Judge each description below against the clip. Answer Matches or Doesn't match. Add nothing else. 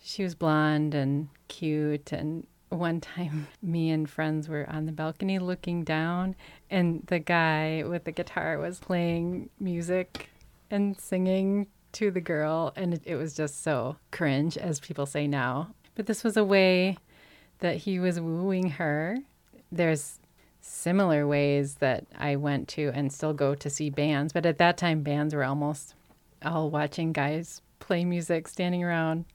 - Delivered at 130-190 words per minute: Matches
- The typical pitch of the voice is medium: Matches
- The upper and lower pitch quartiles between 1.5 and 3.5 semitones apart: Matches